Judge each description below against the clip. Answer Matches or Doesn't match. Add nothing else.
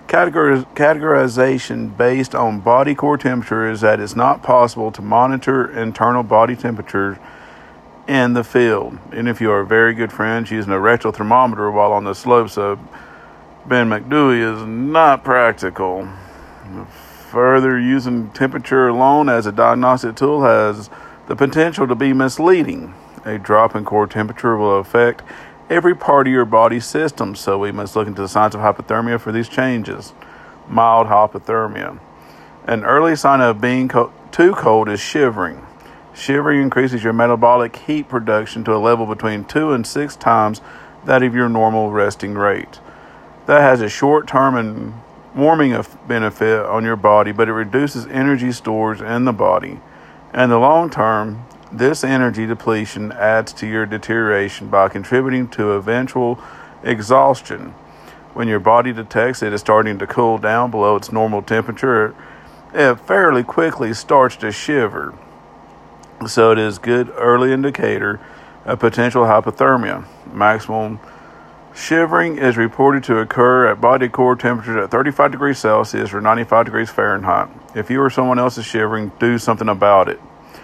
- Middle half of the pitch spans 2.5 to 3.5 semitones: Matches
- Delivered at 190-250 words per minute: Doesn't match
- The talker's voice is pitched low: Matches